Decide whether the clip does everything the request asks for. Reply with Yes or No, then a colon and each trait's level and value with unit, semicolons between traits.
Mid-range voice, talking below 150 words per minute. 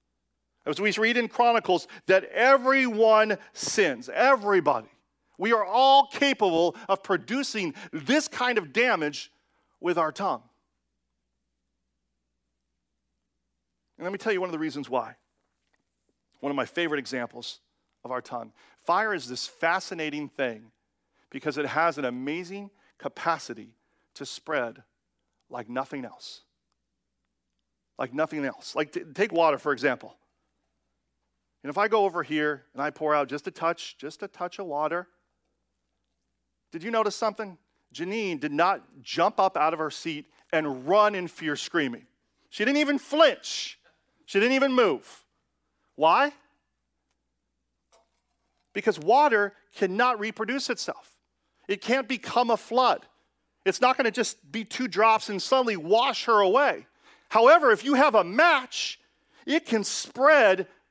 Yes: medium, 175 Hz; average, 140 wpm